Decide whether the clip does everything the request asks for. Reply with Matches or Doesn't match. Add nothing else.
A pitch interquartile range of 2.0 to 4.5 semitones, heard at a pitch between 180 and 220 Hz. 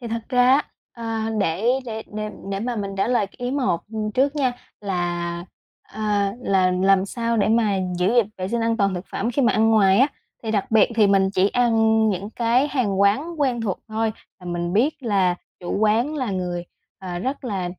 Matches